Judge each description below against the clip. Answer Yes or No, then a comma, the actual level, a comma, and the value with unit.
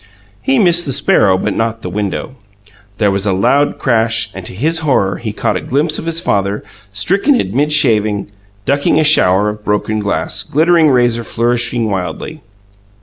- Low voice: Yes, low, 115 Hz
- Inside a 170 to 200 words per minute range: Yes, average, 175 wpm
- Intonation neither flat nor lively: No, wide, 6.5 semitones